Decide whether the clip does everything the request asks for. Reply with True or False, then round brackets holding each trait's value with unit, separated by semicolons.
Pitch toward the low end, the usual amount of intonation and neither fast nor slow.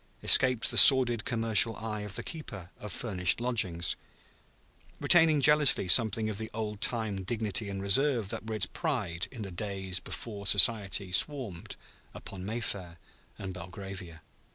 True (105 Hz; 3.6 semitones; 145 wpm)